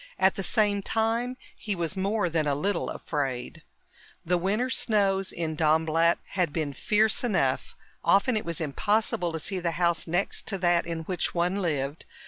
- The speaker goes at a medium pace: Yes, average, 170 wpm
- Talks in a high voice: No, medium, 180 Hz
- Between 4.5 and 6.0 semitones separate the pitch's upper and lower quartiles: No, average, 4.0 semitones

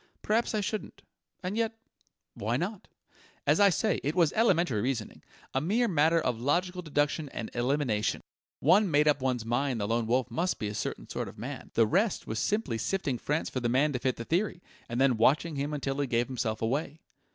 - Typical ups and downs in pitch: No, wide, 6.8 semitones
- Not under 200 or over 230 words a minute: Yes, fast, 205 wpm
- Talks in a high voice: No, medium, 145 Hz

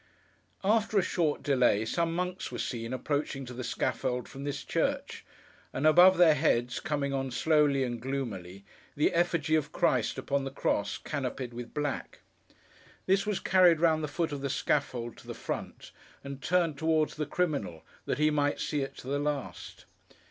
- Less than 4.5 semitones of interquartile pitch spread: Yes, average, 3.7 semitones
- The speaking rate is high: No, average, 175 wpm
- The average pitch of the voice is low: No, medium, 145 Hz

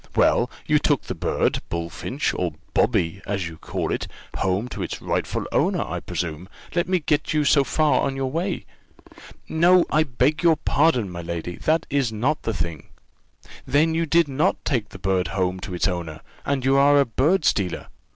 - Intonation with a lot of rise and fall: Yes, wide, 9.0 semitones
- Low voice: Yes, low, 130 Hz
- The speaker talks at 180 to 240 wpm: Yes, average, 190 wpm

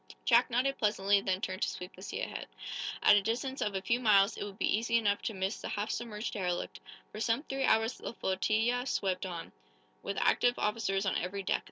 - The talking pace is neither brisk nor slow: No, fast, 215 wpm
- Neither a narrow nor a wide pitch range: Yes, average, 3.2 semitones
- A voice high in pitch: Yes, high, 210 Hz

